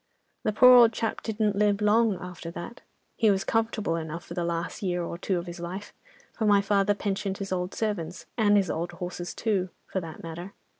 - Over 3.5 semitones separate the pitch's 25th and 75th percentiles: No, average, 3.2 semitones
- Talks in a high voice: Yes, high, 195 Hz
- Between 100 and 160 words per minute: No, fast, 205 wpm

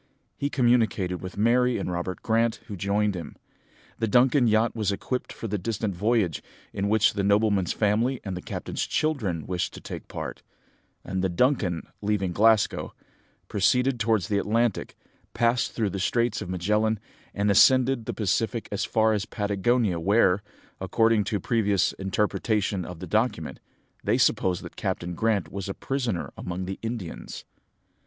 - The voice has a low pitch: Yes, low, 105 Hz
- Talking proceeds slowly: No, average, 160 wpm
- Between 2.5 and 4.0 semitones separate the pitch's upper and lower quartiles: Yes, average, 3.3 semitones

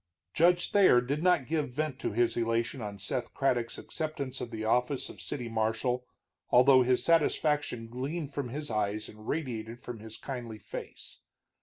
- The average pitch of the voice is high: No, low, 125 Hz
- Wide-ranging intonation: No, average, 4.3 semitones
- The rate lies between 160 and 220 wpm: Yes, average, 165 wpm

